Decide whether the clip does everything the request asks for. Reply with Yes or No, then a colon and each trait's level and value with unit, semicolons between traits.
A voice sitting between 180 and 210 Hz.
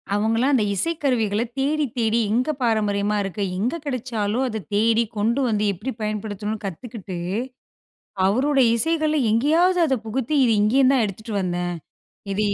No: high, 225 Hz